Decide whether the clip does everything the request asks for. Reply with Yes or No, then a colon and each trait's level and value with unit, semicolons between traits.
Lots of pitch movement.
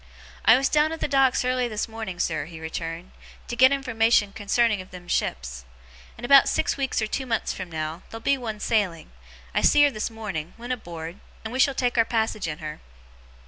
Yes: wide, 6.2 semitones